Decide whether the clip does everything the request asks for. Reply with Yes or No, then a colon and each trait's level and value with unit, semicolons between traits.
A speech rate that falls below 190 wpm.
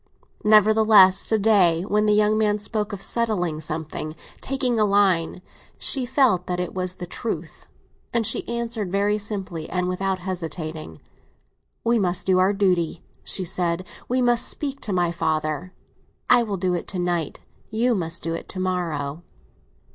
Yes: average, 160 wpm